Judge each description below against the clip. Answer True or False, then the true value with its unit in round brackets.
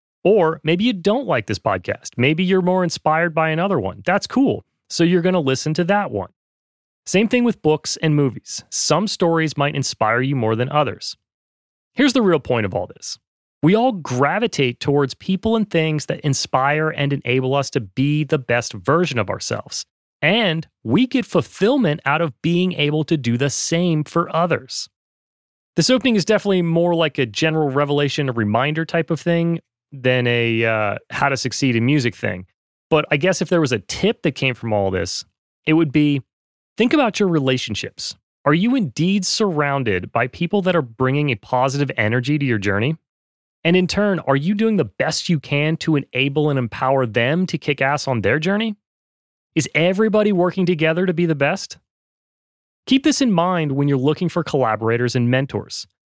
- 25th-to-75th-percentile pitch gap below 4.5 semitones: False (5.4 semitones)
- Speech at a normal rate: True (190 wpm)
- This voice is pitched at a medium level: True (155 Hz)